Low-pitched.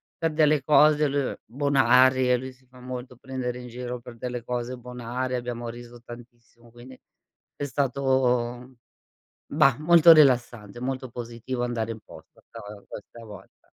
Yes: low, 125 Hz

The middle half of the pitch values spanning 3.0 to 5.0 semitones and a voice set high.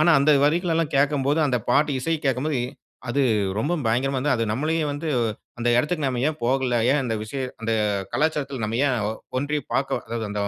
No: average, 3.5 semitones; medium, 140 Hz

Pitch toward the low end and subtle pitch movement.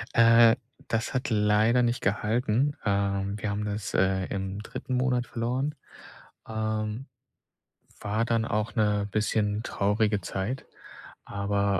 Yes: low, 110 Hz; narrow, 2.3 semitones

